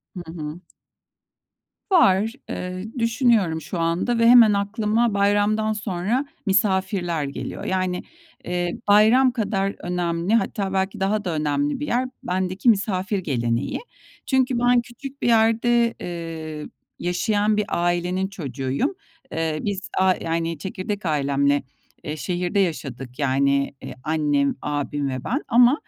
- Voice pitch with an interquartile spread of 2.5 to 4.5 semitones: No, average, 5.1 semitones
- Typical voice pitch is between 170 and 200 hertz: Yes, high, 190 Hz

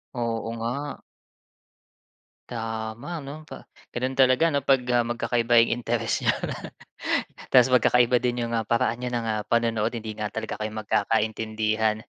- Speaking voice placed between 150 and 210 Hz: No, low, 115 Hz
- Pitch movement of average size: No, narrow, 2.0 semitones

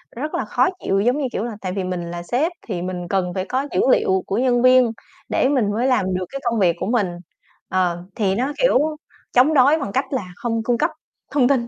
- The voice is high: Yes, high, 230 Hz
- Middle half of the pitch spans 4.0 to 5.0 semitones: No, wide, 5.5 semitones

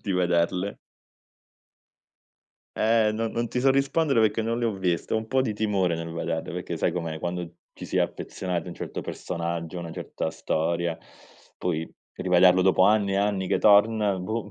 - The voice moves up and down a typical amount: Yes, average, 4.2 semitones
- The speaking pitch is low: Yes, very low, 95 Hz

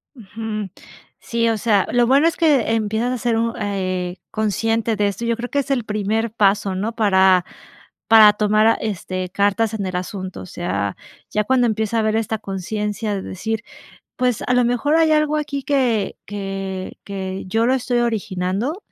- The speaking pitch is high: Yes, high, 220 Hz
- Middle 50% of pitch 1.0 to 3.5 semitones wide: Yes, average, 3.2 semitones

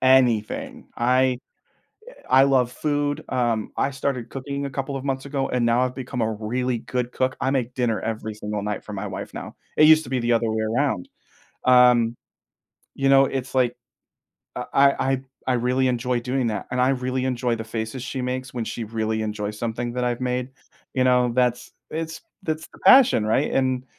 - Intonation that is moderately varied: No, narrow, 2.2 semitones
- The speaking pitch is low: Yes, low, 125 Hz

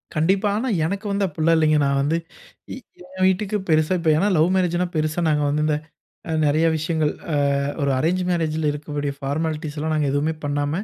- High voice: No, medium, 155 Hz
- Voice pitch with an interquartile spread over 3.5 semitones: No, average, 2.8 semitones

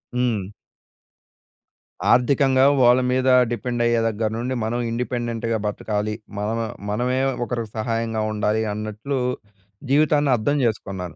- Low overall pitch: Yes, low, 115 Hz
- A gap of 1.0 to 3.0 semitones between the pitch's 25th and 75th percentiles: Yes, narrow, 2.6 semitones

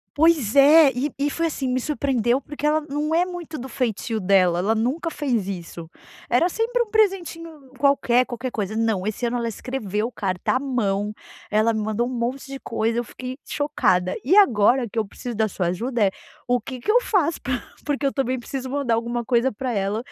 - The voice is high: Yes, very high, 250 Hz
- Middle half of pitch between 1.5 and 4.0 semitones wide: No, average, 4.8 semitones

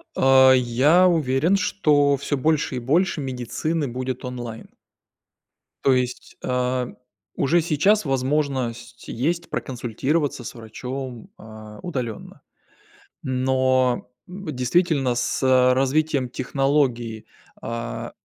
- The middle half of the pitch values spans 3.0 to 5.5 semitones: Yes, average, 3.3 semitones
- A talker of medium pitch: No, low, 130 Hz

